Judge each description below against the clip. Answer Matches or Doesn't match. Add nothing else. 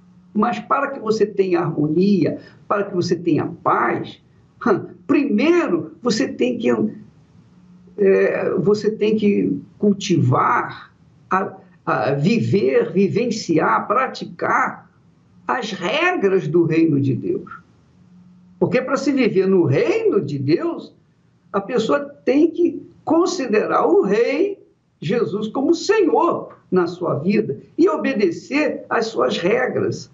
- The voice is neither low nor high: Doesn't match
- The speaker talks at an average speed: Doesn't match